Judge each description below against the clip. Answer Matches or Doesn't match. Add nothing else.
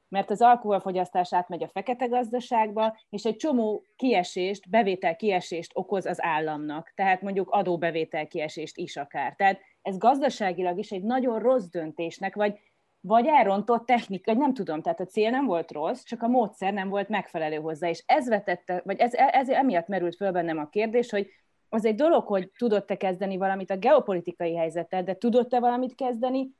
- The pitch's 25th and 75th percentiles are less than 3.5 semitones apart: Doesn't match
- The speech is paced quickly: Matches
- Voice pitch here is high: Matches